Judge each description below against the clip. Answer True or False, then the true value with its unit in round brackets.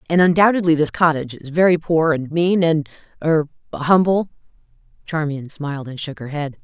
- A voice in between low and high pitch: True (160 Hz)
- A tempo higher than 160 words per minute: False (145 wpm)